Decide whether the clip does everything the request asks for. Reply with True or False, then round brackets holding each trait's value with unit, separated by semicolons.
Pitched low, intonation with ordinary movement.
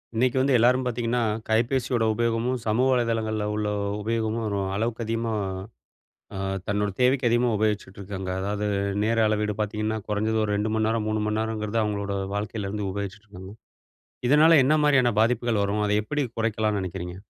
False (110 Hz; 2.2 semitones)